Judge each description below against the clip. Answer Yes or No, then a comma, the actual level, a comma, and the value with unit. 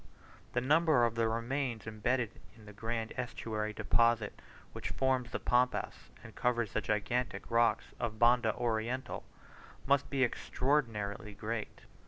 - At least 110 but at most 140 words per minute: Yes, slow, 135 wpm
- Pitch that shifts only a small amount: Yes, narrow, 2.3 semitones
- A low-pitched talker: Yes, low, 115 Hz